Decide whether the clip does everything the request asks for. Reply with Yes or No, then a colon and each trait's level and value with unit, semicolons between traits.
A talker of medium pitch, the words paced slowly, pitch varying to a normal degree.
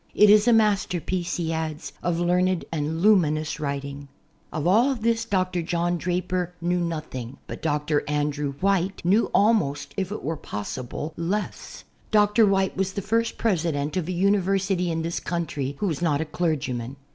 No: medium, 175 Hz; average, 170 wpm; average, 4.2 semitones